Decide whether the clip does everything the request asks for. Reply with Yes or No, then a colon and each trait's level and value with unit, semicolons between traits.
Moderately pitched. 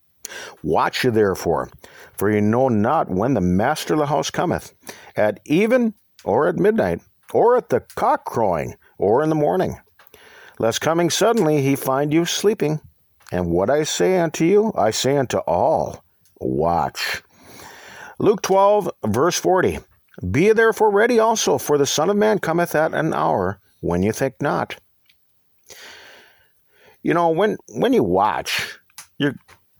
Yes: medium, 155 Hz